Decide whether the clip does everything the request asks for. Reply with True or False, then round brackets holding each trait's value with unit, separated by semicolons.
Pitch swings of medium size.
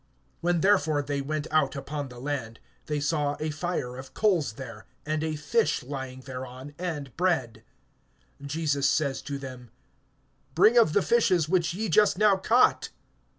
True (4.6 semitones)